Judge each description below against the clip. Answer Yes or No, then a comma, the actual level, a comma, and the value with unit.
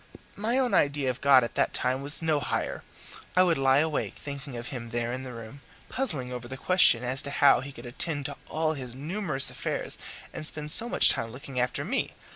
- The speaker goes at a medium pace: No, fast, 220 wpm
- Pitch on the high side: No, medium, 140 Hz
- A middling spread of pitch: Yes, average, 3.7 semitones